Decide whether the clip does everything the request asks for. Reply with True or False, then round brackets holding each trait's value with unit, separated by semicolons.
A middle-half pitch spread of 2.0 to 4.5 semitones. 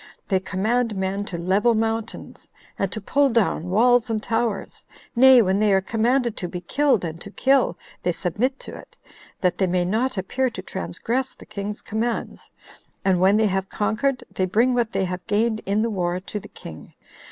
True (4.0 semitones)